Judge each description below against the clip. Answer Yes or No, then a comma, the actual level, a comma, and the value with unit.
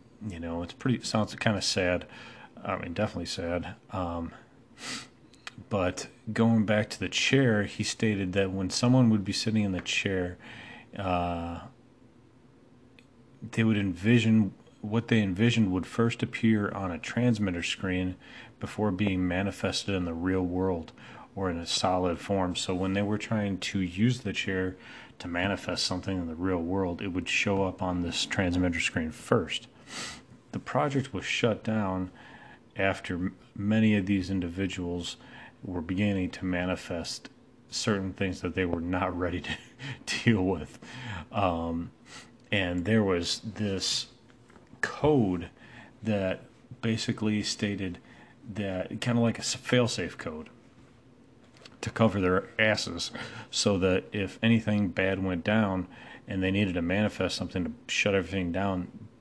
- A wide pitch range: No, average, 4.0 semitones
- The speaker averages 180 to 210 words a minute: No, average, 145 wpm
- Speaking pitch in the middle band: No, low, 100 Hz